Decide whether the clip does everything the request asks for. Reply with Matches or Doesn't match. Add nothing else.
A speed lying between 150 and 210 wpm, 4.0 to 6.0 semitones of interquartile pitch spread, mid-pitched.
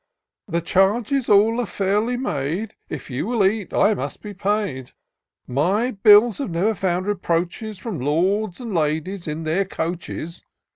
Doesn't match